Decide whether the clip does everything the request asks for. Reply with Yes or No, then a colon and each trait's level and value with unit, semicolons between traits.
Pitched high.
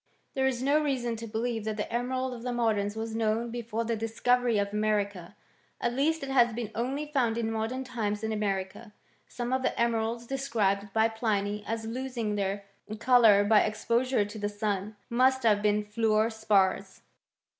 Yes: high, 225 Hz